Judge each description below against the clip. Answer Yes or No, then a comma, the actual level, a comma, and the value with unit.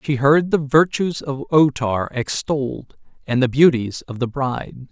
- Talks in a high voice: No, low, 135 Hz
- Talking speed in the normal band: Yes, average, 170 wpm